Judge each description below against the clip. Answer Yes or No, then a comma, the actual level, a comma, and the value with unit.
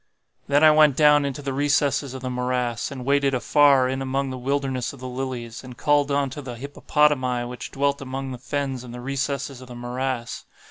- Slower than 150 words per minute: No, average, 200 wpm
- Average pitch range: No, narrow, 1.9 semitones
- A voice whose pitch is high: No, low, 135 Hz